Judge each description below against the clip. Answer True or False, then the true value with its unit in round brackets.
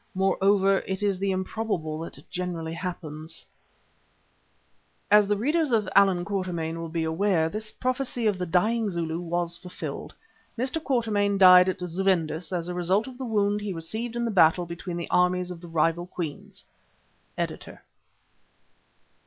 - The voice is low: False (185 Hz)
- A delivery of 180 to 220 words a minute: False (155 wpm)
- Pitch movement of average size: True (3.4 semitones)